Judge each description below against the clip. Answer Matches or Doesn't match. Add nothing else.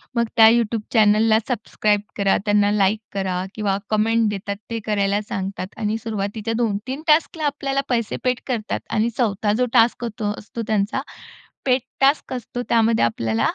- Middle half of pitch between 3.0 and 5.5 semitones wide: Doesn't match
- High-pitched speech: Matches